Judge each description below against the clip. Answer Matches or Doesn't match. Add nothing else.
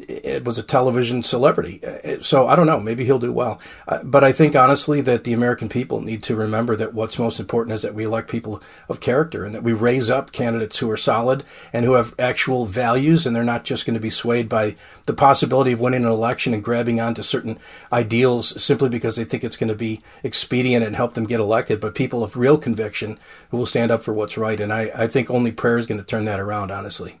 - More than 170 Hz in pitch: Doesn't match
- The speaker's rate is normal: Doesn't match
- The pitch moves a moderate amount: Doesn't match